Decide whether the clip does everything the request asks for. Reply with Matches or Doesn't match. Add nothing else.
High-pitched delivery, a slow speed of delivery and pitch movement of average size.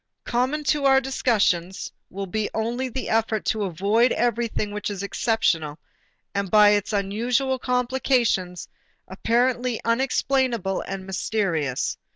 Matches